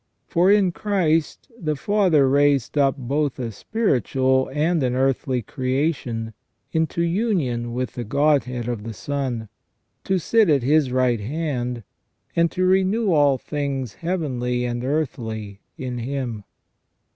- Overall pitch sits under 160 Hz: Yes, low, 135 Hz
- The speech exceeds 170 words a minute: No, slow, 135 wpm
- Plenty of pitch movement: No, average, 4.9 semitones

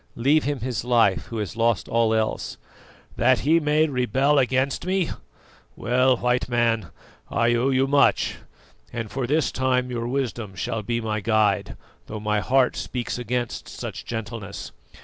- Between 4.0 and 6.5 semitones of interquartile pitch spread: No, average, 2.8 semitones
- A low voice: Yes, low, 120 Hz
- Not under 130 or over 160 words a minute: Yes, average, 155 wpm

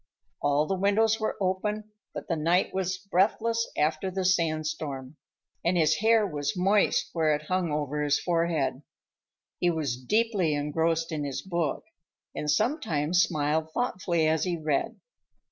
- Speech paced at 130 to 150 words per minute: Yes, average, 145 wpm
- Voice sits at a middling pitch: Yes, medium, 165 Hz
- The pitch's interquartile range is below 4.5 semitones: Yes, average, 4.0 semitones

